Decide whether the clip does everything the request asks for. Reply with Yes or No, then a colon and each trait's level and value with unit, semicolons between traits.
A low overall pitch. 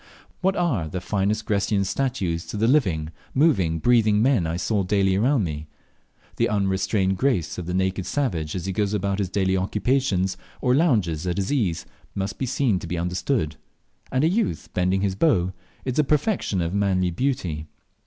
Yes: low, 100 Hz